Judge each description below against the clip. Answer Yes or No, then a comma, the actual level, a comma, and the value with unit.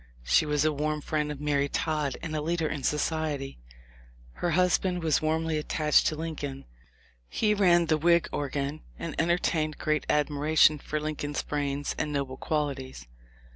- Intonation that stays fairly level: Yes, narrow, 1.7 semitones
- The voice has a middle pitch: Yes, medium, 150 Hz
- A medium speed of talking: Yes, average, 160 wpm